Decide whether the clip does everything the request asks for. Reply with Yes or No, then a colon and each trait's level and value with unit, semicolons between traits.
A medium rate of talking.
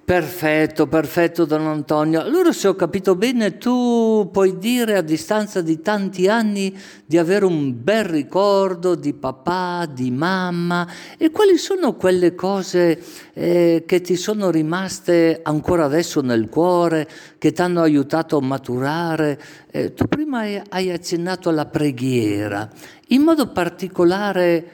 Yes: average, 135 wpm